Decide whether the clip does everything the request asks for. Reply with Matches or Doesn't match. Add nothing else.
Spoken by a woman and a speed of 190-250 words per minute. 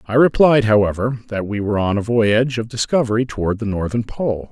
Doesn't match